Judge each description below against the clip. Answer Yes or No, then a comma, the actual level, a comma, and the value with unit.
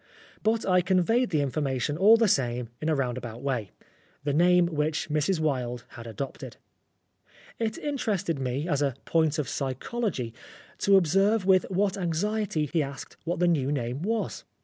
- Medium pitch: Yes, medium, 155 Hz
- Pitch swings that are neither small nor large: No, wide, 6.1 semitones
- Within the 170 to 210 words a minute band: No, average, 160 wpm